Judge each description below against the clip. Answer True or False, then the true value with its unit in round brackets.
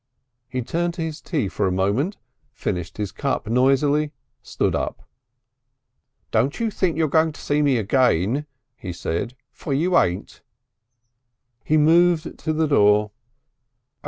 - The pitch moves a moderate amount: False (6.9 semitones)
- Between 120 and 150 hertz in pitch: True (140 Hz)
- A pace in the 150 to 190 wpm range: False (140 wpm)